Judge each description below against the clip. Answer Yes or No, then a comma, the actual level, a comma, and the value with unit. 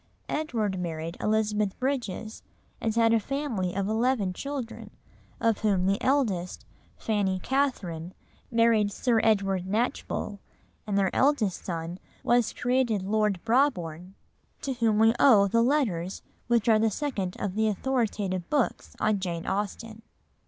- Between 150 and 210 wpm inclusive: No, slow, 135 wpm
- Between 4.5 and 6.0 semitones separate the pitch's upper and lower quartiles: No, average, 4.0 semitones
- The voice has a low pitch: No, high, 215 Hz